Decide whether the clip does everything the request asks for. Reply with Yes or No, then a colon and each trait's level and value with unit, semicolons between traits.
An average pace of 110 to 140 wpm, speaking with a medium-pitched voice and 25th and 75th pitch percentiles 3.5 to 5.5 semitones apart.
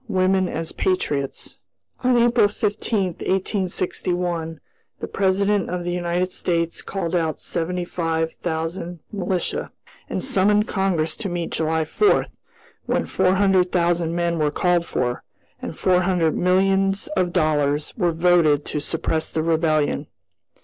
No: slow, 135 wpm; medium, 175 Hz; average, 2.8 semitones